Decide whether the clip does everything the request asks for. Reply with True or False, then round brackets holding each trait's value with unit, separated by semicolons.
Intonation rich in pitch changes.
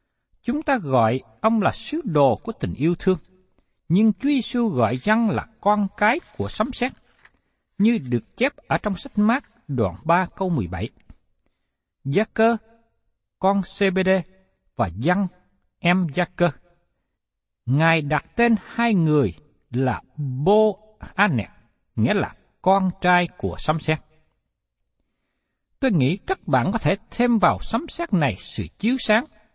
True (6.3 semitones)